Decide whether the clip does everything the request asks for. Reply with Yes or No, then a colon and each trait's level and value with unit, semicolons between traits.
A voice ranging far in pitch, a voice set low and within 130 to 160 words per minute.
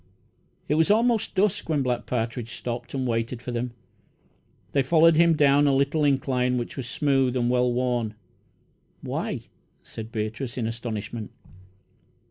No: average, 3.4 semitones; low, 125 Hz; average, 145 wpm